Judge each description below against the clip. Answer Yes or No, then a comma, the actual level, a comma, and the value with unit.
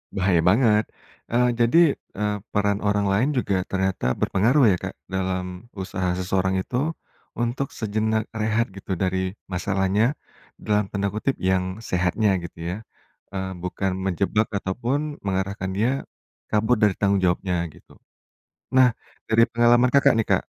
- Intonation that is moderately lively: Yes, average, 3.3 semitones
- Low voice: Yes, low, 100 Hz